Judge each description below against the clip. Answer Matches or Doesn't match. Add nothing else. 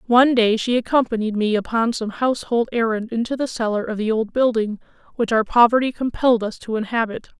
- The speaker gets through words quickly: Doesn't match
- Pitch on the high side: Matches